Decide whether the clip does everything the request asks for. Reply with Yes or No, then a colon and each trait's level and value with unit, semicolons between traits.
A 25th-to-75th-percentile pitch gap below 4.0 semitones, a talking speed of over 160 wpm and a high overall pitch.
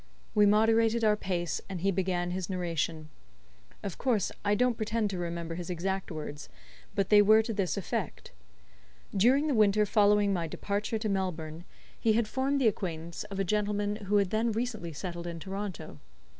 Yes: average, 3.6 semitones; average, 175 wpm; high, 200 Hz